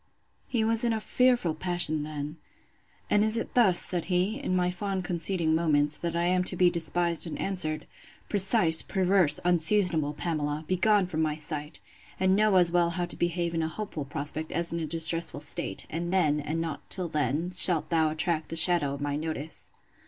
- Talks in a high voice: No, medium, 170 Hz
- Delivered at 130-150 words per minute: No, average, 190 wpm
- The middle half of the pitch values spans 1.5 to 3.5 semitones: Yes, average, 2.9 semitones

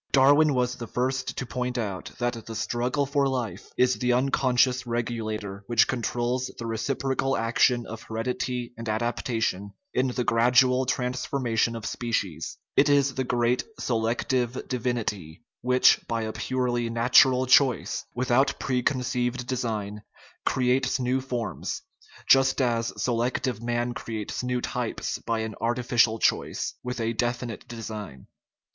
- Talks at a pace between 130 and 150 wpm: Yes, average, 140 wpm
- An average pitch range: No, narrow, 1.8 semitones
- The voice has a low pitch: Yes, low, 120 Hz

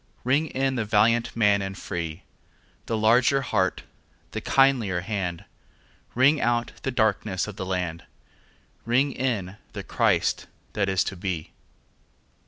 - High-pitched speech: No, low, 110 Hz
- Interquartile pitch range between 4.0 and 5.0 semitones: Yes, average, 4.7 semitones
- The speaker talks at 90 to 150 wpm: Yes, slow, 135 wpm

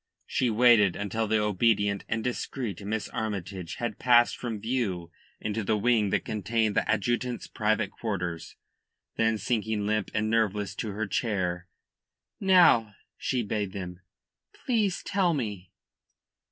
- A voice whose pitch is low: Yes, low, 110 Hz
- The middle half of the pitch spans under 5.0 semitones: Yes, average, 2.8 semitones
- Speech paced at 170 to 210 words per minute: No, slow, 135 wpm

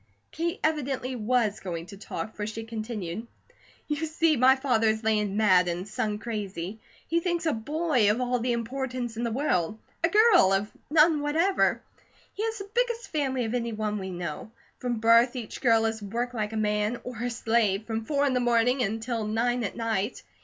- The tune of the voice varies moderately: Yes, average, 3.9 semitones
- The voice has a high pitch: Yes, high, 230 Hz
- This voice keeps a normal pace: Yes, average, 195 wpm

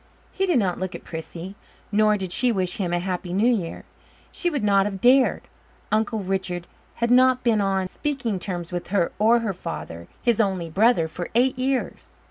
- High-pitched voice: Yes, high, 200 Hz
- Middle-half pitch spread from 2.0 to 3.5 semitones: No, average, 4.9 semitones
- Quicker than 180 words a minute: Yes, average, 190 wpm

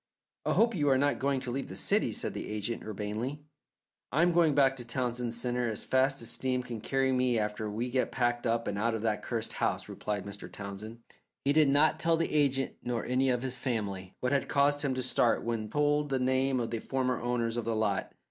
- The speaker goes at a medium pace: No, fast, 235 wpm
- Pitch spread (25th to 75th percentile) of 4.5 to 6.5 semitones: No, average, 3.0 semitones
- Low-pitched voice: Yes, low, 125 Hz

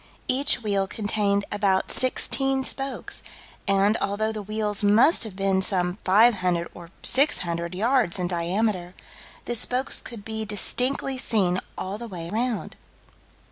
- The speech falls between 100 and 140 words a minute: Yes, slow, 135 wpm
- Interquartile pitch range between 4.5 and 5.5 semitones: No, average, 3.8 semitones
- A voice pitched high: Yes, high, 205 Hz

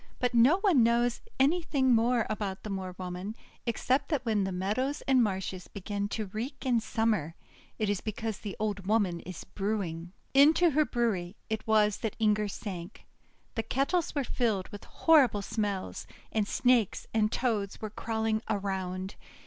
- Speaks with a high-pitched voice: Yes, high, 215 Hz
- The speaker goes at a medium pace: Yes, average, 160 wpm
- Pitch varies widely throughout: No, average, 3.7 semitones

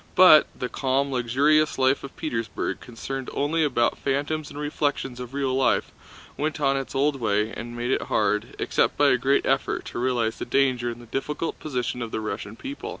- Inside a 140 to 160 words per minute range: No, average, 200 wpm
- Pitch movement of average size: Yes, average, 3.4 semitones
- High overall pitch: No, low, 135 Hz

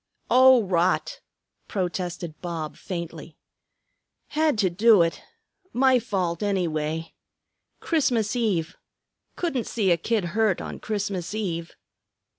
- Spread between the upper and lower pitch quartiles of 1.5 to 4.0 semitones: No, average, 5.2 semitones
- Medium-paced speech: No, slow, 105 wpm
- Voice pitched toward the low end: No, high, 190 Hz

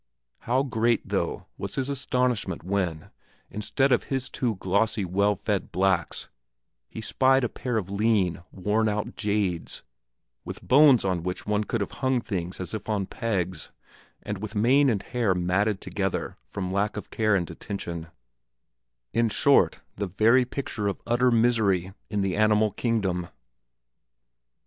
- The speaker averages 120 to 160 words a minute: Yes, average, 150 wpm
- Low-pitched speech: Yes, low, 105 Hz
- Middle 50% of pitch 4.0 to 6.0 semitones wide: No, average, 3.6 semitones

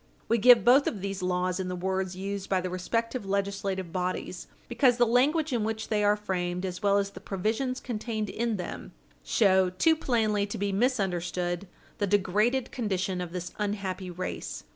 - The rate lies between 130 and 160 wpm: No, average, 180 wpm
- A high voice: Yes, high, 200 Hz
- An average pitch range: Yes, average, 3.5 semitones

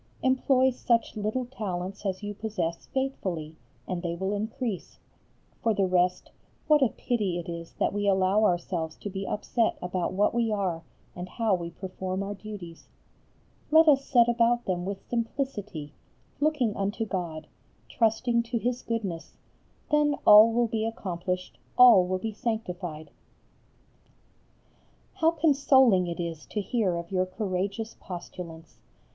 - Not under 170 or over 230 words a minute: No, average, 145 wpm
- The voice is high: Yes, high, 205 Hz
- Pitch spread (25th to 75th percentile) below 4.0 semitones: No, average, 4.5 semitones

